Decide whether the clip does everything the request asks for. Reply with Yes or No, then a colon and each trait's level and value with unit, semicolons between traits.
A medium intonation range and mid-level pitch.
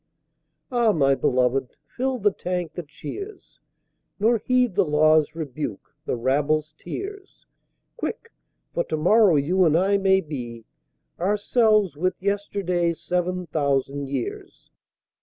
No: wide, 5.7 semitones; medium, 175 Hz